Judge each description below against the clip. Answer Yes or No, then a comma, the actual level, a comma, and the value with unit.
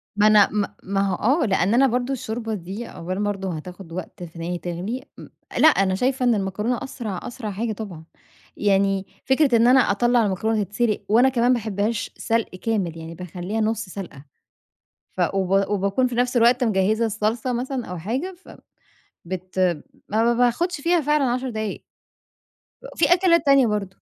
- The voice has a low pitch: No, high, 215 Hz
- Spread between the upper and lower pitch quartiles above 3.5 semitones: Yes, average, 4.2 semitones